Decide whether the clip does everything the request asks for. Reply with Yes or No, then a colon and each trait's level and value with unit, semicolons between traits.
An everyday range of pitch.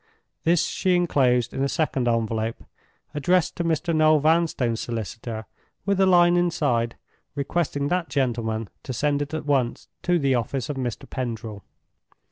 No: wide, 6.0 semitones